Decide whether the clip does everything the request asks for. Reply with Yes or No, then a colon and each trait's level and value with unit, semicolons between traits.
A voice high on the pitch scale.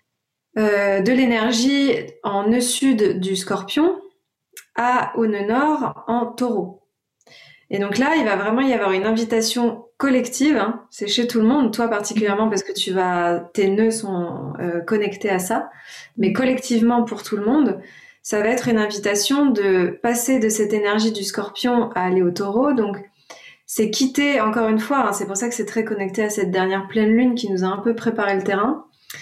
Yes: high, 220 Hz